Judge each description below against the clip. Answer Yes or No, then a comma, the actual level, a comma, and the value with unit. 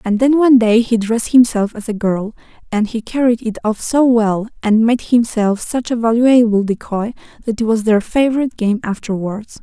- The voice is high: Yes, high, 225 Hz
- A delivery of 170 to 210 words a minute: Yes, average, 195 wpm